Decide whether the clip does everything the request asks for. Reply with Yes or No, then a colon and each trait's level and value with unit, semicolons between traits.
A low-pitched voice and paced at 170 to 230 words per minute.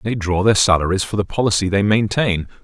Yes: low, 100 Hz; fast, 205 wpm